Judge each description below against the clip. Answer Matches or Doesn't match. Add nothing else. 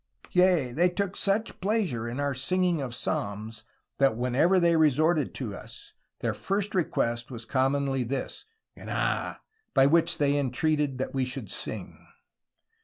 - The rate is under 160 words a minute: Matches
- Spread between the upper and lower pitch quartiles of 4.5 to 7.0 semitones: Matches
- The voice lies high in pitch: Doesn't match